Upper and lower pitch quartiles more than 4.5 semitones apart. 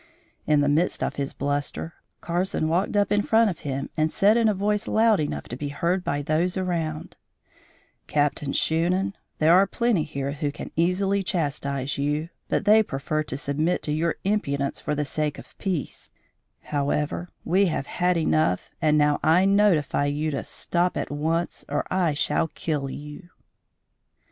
No: average, 4.1 semitones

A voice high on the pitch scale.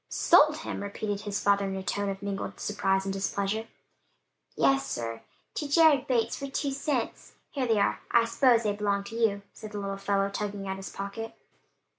Yes: high, 205 Hz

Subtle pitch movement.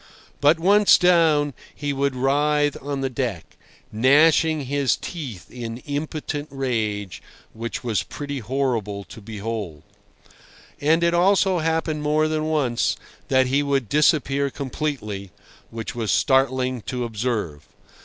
No: average, 4.6 semitones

